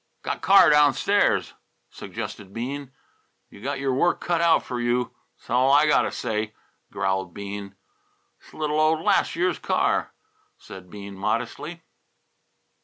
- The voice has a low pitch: Yes, low, 130 Hz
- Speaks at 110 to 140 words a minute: Yes, slow, 135 wpm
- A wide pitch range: Yes, wide, 7.1 semitones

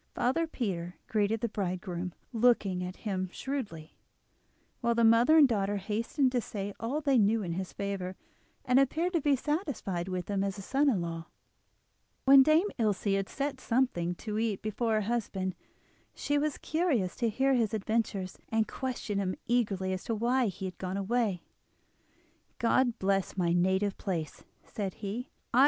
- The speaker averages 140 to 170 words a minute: Yes, average, 165 wpm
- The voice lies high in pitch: Yes, high, 215 Hz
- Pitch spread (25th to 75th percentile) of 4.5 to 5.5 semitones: Yes, average, 4.8 semitones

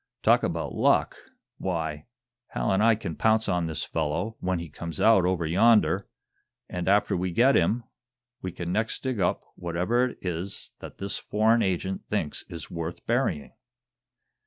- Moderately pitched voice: No, very low, 95 Hz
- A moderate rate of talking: Yes, average, 160 wpm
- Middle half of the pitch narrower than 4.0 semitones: No, average, 4.6 semitones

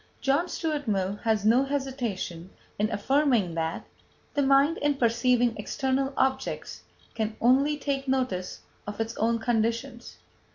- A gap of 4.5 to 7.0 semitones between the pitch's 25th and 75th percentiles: No, average, 3.9 semitones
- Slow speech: Yes, slow, 130 wpm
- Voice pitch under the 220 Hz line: No, high, 245 Hz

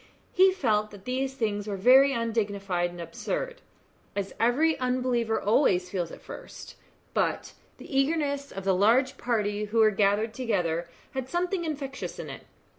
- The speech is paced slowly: No, average, 155 wpm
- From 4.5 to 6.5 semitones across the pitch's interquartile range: Yes, average, 5.0 semitones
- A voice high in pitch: Yes, high, 230 Hz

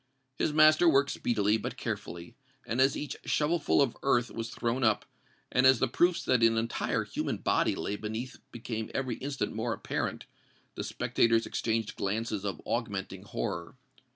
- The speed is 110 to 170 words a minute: Yes, average, 165 wpm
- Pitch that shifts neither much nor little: Yes, average, 3.4 semitones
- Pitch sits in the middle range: No, low, 115 Hz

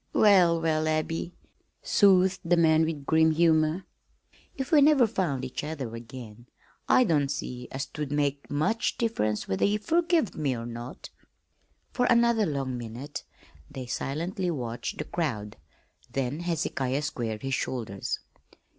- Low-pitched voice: No, medium, 155 Hz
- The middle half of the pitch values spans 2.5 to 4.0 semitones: No, wide, 5.6 semitones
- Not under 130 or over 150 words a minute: Yes, average, 140 wpm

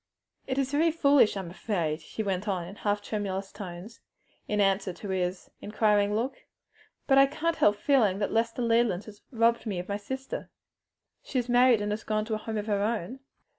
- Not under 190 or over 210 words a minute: Yes, average, 200 wpm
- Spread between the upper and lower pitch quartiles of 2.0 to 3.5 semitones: Yes, average, 3.2 semitones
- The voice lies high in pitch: Yes, high, 210 Hz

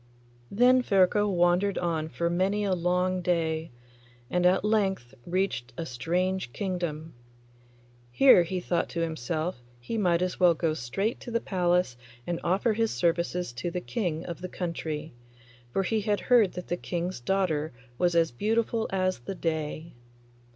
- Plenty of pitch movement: No, average, 2.8 semitones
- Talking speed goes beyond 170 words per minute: No, average, 160 wpm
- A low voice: No, medium, 180 Hz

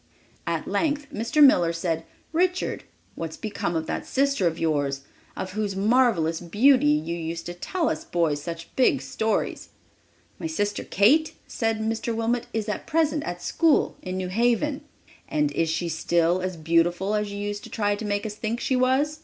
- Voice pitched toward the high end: Yes, high, 205 Hz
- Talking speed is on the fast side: No, average, 180 wpm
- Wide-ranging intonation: Yes, wide, 6.6 semitones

